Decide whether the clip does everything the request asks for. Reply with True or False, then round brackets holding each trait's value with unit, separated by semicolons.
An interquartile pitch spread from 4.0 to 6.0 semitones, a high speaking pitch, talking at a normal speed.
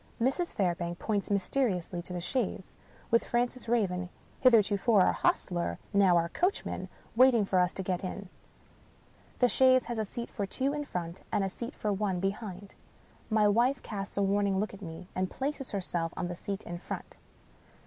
True (4.6 semitones; 200 Hz; 180 wpm)